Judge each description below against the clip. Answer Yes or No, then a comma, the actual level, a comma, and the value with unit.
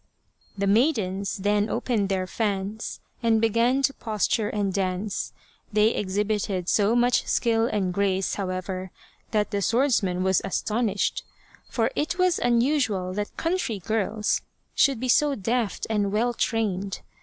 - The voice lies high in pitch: Yes, high, 210 Hz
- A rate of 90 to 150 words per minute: Yes, average, 140 wpm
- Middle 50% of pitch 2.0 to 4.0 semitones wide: Yes, average, 3.3 semitones